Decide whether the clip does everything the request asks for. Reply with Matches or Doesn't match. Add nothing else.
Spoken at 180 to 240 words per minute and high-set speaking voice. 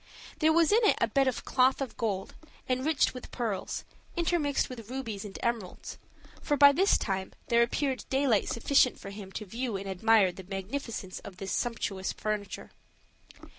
Doesn't match